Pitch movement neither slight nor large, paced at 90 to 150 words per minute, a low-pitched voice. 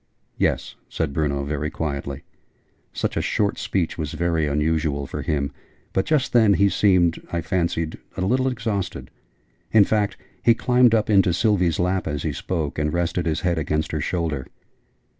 No: average, 4.7 semitones; average, 165 wpm; very low, 85 Hz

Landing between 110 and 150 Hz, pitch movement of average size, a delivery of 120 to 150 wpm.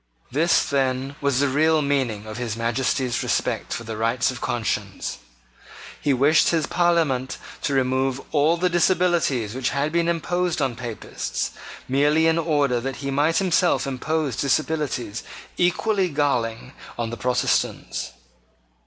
Yes: medium, 140 Hz; average, 4.4 semitones; slow, 135 wpm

